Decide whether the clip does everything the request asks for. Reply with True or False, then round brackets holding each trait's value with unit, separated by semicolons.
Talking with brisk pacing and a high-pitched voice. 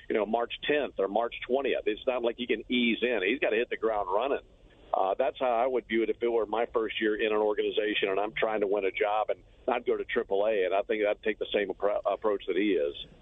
True (275 wpm; 390 Hz)